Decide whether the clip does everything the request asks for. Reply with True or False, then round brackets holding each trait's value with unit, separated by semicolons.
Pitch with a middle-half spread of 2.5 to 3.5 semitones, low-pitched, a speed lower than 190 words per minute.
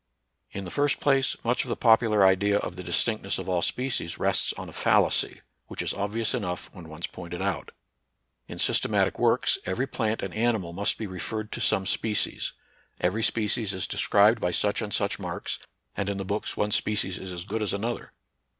False (3.2 semitones; 100 Hz; 195 wpm)